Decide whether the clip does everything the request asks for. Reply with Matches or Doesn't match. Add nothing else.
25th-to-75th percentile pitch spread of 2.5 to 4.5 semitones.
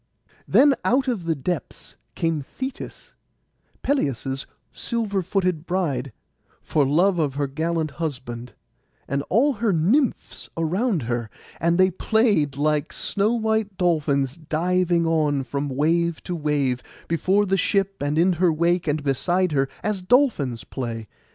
Doesn't match